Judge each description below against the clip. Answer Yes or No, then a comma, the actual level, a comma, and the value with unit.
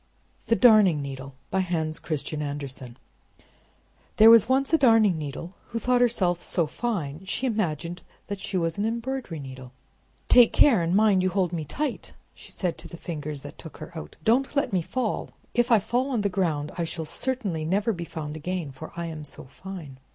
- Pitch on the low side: No, medium, 180 Hz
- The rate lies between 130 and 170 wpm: No, average, 190 wpm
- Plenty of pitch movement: Yes, wide, 6.6 semitones